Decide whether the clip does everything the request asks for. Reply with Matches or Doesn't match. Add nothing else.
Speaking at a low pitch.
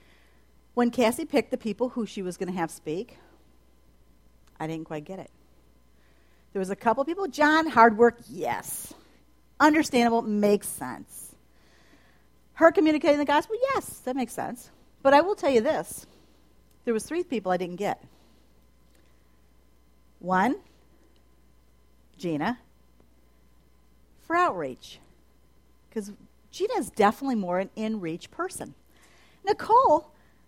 Doesn't match